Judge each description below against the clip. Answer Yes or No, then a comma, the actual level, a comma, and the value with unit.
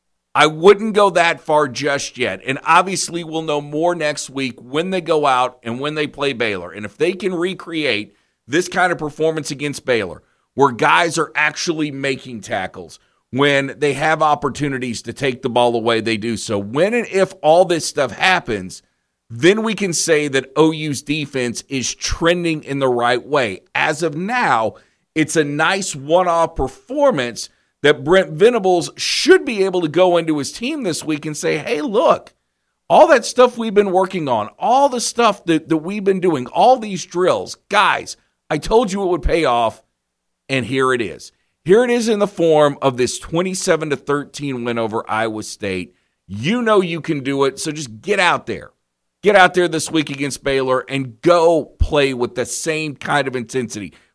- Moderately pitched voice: Yes, medium, 155 Hz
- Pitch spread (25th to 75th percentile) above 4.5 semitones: Yes, wide, 5.5 semitones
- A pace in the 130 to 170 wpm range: No, average, 190 wpm